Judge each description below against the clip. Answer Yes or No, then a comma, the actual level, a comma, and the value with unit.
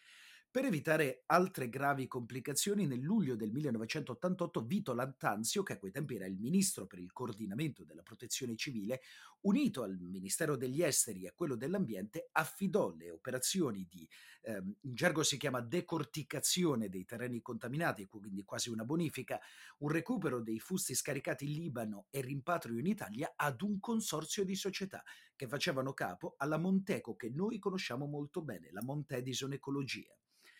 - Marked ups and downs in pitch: Yes, wide, 6.4 semitones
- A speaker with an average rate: Yes, average, 155 wpm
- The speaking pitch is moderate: Yes, medium, 145 Hz